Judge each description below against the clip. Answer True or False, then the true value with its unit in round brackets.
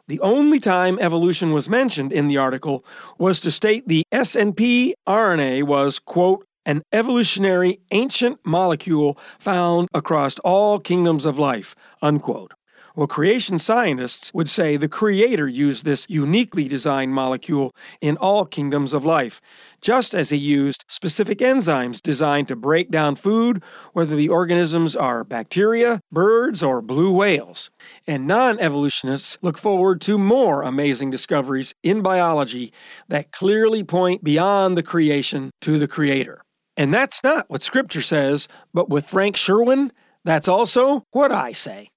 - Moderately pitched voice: True (170 Hz)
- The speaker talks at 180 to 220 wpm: False (145 wpm)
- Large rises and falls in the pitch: True (6.1 semitones)